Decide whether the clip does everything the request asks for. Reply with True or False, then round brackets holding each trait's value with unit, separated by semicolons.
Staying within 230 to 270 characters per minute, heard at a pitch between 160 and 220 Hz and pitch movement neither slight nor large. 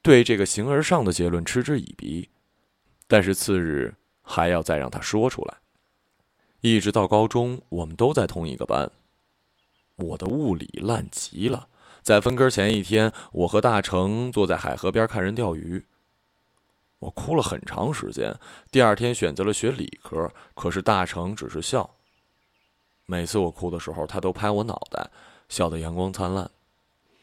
False (235 characters per minute; 100 Hz; 3.9 semitones)